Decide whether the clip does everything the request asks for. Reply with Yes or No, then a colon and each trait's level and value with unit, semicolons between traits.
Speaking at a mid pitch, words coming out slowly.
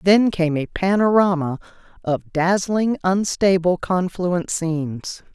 Yes: medium, 180 Hz; slow, 100 wpm